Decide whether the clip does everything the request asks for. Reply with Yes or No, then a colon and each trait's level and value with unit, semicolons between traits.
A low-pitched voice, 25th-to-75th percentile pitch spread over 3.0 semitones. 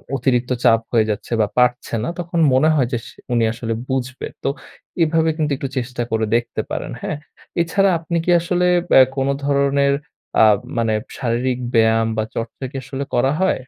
Yes: low, 130 Hz; average, 3.4 semitones